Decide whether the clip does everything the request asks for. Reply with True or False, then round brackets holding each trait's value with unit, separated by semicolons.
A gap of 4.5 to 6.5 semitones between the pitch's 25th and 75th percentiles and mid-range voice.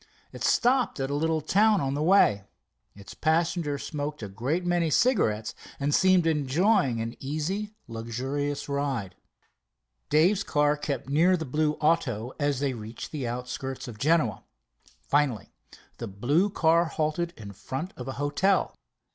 True (4.9 semitones; 145 Hz)